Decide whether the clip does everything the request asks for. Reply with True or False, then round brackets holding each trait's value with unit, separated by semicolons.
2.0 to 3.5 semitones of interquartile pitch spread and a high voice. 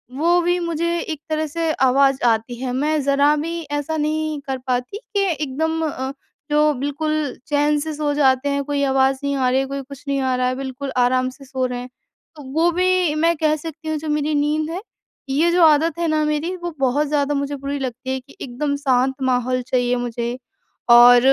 True (3.0 semitones; 285 Hz)